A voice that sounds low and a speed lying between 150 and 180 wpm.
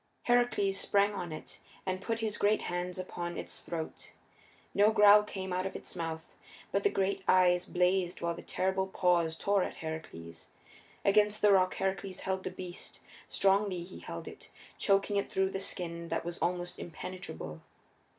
No: medium, 185 Hz; average, 170 wpm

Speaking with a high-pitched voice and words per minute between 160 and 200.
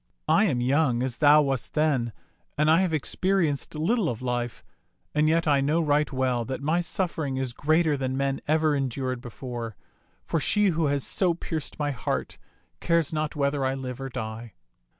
No: medium, 145 Hz; average, 180 wpm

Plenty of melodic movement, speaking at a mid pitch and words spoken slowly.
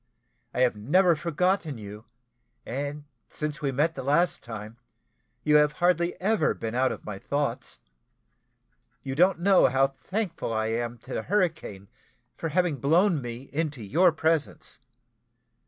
No: wide, 6.0 semitones; medium, 145 Hz; average, 145 wpm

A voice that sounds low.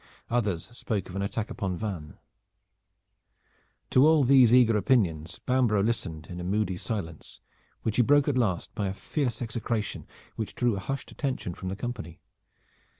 Yes: low, 110 Hz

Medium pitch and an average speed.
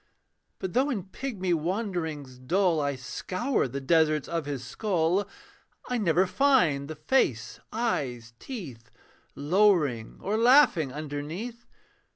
No: medium, 170 Hz; slow, 120 wpm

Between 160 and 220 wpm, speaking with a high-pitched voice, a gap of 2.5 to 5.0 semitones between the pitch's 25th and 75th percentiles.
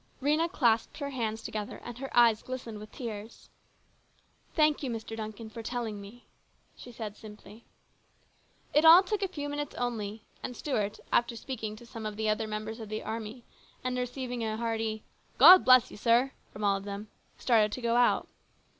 Yes: average, 190 wpm; high, 230 Hz; average, 2.9 semitones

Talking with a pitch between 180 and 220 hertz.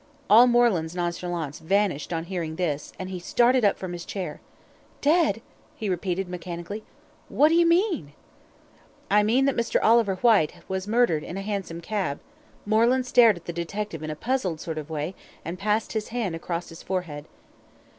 Yes: high, 190 Hz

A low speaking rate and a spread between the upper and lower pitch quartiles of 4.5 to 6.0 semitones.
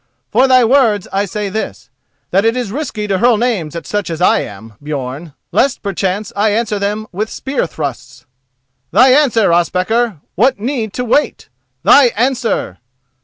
No: average, 165 wpm; average, 5.2 semitones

